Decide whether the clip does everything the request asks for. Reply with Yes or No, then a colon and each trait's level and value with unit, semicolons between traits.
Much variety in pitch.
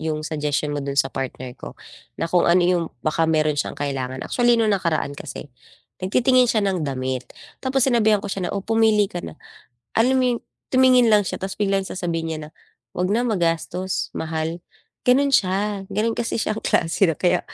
Yes: wide, 5.7 semitones